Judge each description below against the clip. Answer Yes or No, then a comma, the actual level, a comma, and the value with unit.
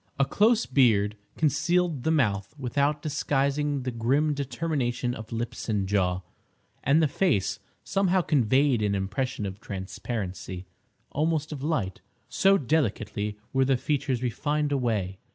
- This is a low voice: Yes, low, 130 Hz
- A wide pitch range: Yes, wide, 6.1 semitones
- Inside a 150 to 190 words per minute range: No, slow, 135 wpm